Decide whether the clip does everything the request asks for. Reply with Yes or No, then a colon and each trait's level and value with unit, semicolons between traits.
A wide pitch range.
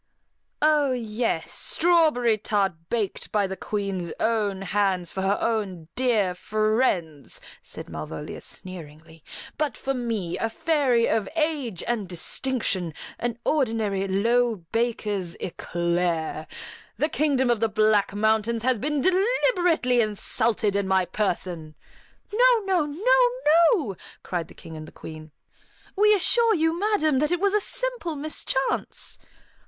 Yes: wide, 7.9 semitones